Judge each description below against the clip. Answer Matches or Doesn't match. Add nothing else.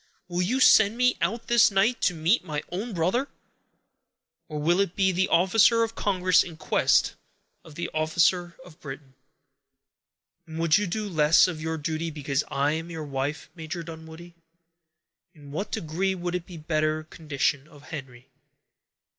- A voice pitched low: Doesn't match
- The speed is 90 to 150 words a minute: Doesn't match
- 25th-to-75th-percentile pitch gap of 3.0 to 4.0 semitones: Matches